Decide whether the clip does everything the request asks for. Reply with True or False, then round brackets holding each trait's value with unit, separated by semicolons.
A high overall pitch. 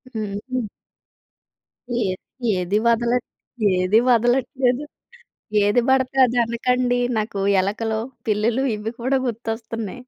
True (230 Hz)